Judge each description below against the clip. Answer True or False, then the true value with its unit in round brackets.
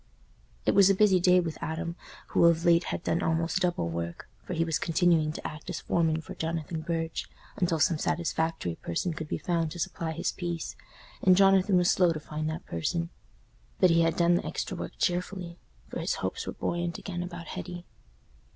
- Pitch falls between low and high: True (170 Hz)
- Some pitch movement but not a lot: False (1.7 semitones)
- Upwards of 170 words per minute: True (195 wpm)